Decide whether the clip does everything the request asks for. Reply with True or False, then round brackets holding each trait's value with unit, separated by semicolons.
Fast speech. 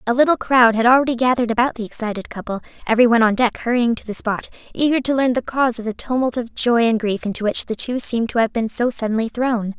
True (250 wpm)